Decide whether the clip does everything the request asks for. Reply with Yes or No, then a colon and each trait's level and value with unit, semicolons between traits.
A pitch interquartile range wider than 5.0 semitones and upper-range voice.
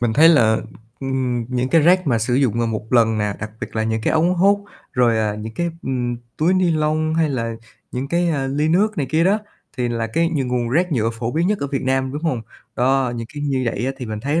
No: wide, 5.4 semitones; low, 130 Hz